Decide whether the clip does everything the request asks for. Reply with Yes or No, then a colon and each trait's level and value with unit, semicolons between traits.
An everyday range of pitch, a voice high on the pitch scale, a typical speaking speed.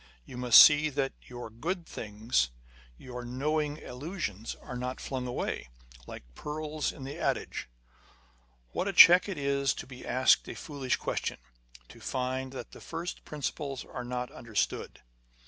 No: average, 3.4 semitones; low, 130 Hz; average, 160 wpm